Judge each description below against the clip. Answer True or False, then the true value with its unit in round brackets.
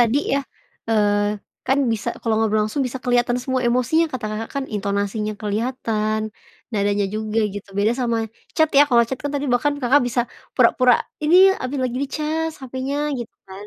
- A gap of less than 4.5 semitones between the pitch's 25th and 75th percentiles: True (3.6 semitones)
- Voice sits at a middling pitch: False (240 Hz)